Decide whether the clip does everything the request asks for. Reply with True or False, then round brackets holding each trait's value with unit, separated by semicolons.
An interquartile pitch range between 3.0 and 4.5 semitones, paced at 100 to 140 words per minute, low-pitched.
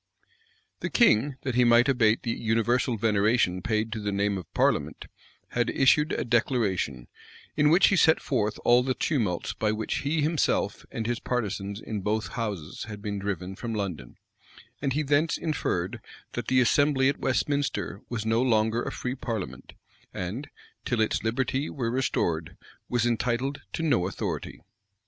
False (4.1 semitones; 160 wpm; 115 Hz)